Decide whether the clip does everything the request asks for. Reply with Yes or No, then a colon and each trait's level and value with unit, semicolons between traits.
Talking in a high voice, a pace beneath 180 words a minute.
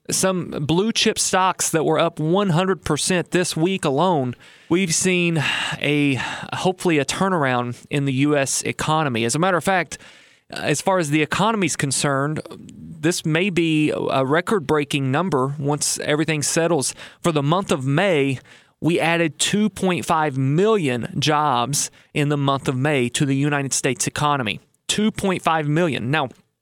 No: medium, 155 Hz; average, 150 wpm